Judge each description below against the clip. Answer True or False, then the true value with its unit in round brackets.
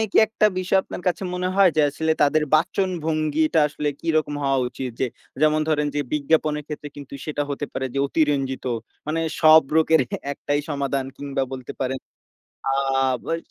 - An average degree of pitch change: False (2.3 semitones)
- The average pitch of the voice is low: False (150 Hz)